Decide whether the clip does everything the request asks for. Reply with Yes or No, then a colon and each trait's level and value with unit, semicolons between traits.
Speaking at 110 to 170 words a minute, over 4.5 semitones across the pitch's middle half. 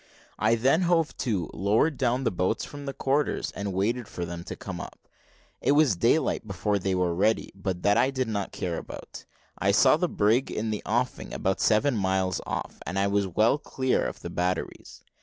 No: average, 200 wpm; average, 5.2 semitones